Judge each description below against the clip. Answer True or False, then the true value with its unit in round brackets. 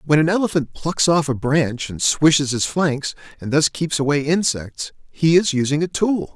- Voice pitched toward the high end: False (150 Hz)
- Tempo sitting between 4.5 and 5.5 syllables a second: True (4.6 syllables/s)